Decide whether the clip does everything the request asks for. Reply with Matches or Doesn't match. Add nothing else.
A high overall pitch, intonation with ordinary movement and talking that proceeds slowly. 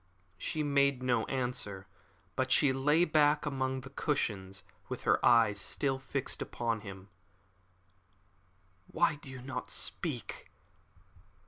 Doesn't match